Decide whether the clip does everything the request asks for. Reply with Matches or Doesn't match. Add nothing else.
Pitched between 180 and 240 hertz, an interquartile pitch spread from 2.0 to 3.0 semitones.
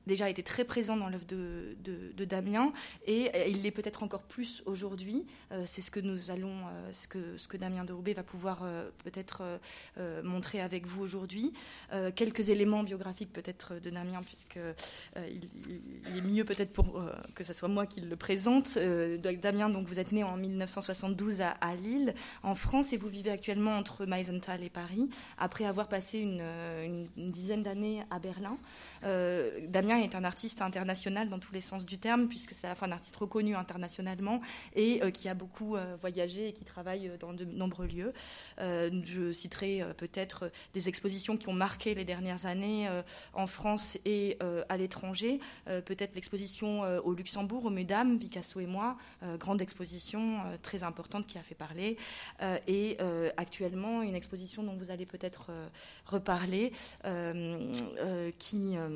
Matches